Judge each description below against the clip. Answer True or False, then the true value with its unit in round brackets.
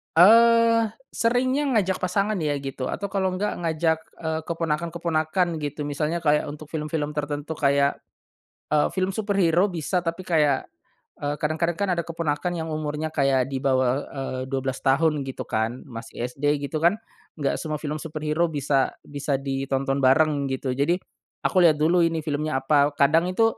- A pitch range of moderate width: True (3.4 semitones)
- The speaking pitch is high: False (155 Hz)